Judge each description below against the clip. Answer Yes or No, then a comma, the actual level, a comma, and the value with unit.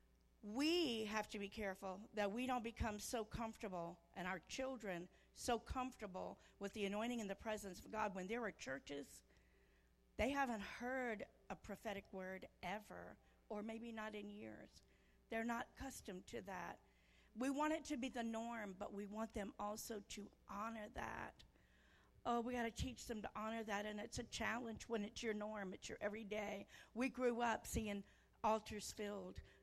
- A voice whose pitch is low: No, high, 215 Hz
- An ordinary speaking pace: Yes, average, 175 wpm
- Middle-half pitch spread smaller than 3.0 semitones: Yes, narrow, 2.6 semitones